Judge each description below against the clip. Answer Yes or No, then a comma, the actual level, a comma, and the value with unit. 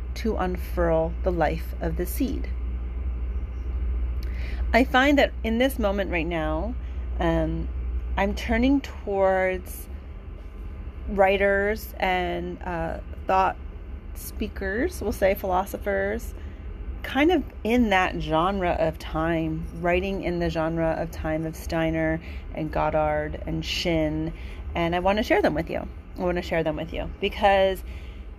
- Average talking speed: No, slow, 130 wpm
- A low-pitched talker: No, medium, 160 Hz